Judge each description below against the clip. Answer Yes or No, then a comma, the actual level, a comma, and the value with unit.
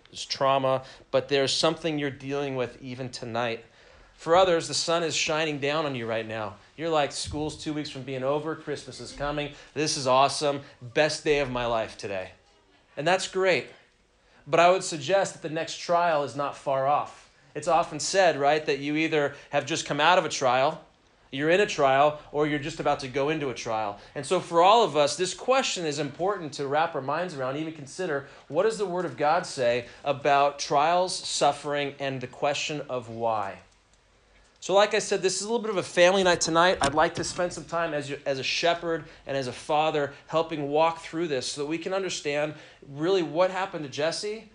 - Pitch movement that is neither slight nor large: Yes, average, 3.7 semitones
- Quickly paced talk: Yes, fast, 215 wpm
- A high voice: No, medium, 150 Hz